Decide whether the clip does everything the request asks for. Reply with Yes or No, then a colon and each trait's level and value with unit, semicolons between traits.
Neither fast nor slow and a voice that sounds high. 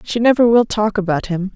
No: fast, 230 wpm; high, 210 Hz